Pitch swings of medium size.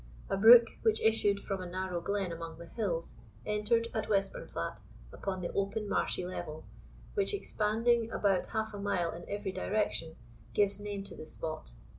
Yes: average, 3.3 semitones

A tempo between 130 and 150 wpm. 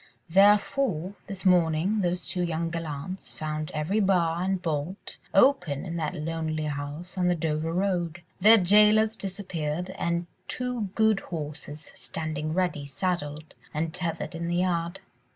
Yes: average, 140 wpm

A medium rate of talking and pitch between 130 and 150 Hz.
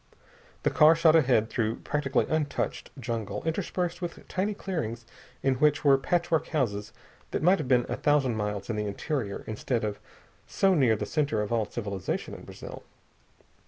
Yes: average, 165 wpm; low, 135 Hz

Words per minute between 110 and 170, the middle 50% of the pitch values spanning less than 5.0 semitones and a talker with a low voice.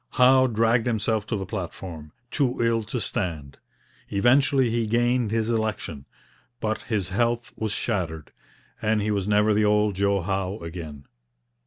Yes: average, 150 wpm; average, 3.4 semitones; low, 105 Hz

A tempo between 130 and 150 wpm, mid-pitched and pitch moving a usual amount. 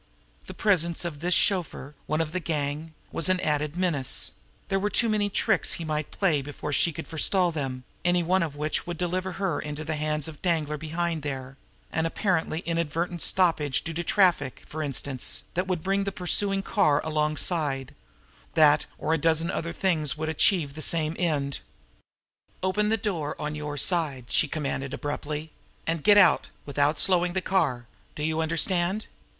No: average, 180 wpm; medium, 160 Hz; average, 3.1 semitones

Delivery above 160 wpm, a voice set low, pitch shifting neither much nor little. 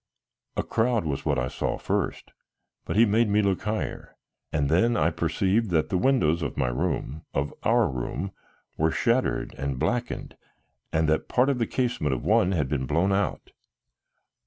No: average, 175 wpm; very low, 90 Hz; wide, 7.6 semitones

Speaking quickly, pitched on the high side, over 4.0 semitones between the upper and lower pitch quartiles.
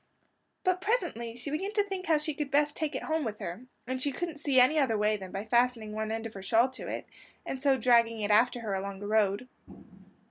Yes: fast, 240 wpm; very high, 250 Hz; wide, 5.5 semitones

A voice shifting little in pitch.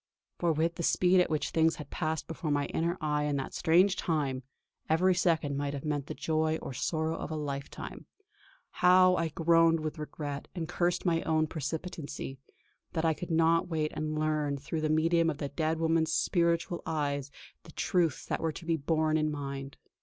Yes: narrow, 1.9 semitones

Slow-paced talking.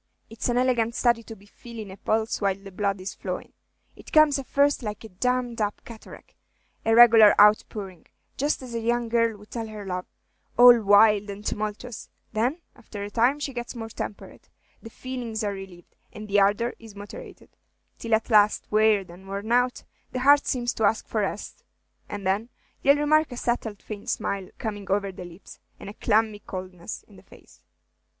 No: average, 190 wpm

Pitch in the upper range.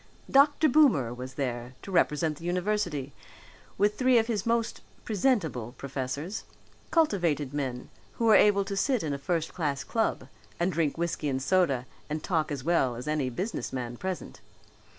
No: medium, 165 Hz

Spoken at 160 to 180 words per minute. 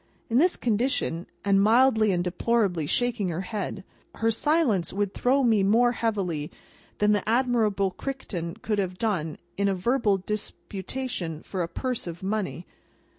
No: average, 150 wpm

